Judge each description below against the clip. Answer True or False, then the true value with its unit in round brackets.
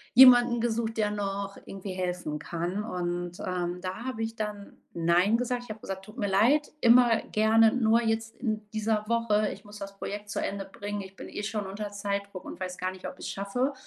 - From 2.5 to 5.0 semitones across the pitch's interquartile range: True (2.8 semitones)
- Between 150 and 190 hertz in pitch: False (205 Hz)